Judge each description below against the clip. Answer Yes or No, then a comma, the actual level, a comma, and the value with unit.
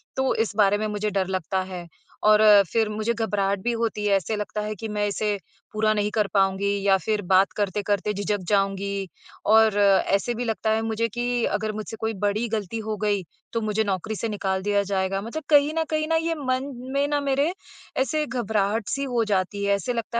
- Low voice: No, high, 210 Hz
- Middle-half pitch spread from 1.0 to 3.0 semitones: Yes, narrow, 2.4 semitones